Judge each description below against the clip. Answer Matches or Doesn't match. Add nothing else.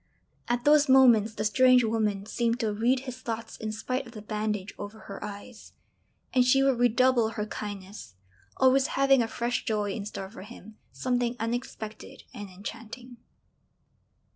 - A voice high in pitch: Matches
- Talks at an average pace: Matches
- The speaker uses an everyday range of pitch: Matches